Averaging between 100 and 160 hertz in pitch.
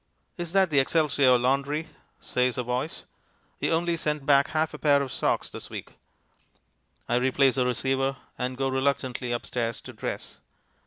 Yes: low, 135 Hz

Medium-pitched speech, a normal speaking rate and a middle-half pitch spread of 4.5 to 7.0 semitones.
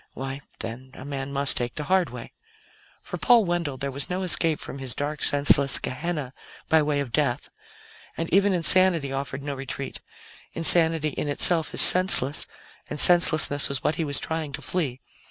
No: medium, 145 Hz; average, 175 wpm; average, 3.4 semitones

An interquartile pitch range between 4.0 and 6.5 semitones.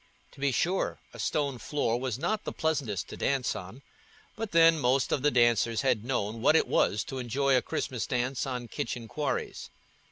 No: average, 3.5 semitones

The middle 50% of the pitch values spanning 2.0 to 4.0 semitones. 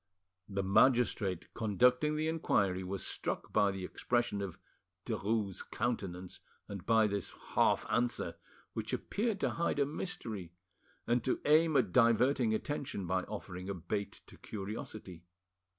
No: average, 4.6 semitones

